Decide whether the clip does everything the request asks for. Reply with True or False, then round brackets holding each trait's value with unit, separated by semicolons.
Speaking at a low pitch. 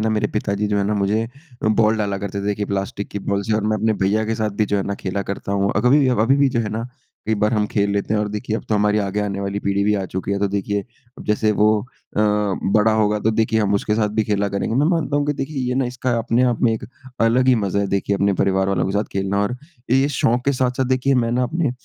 True (105 Hz)